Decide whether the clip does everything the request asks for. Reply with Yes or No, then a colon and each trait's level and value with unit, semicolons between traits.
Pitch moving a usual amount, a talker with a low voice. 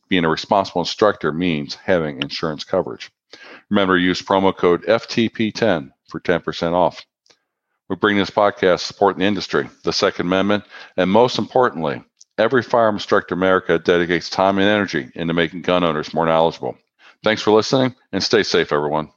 Yes: average, 3.7 semitones; very low, 95 Hz